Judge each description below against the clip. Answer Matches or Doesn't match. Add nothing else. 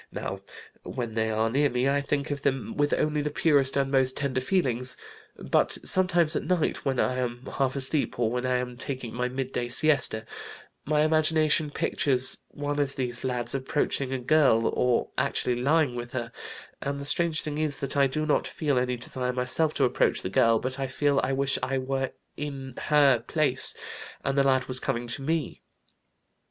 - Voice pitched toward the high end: Doesn't match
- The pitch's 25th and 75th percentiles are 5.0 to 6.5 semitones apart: Doesn't match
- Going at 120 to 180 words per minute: Doesn't match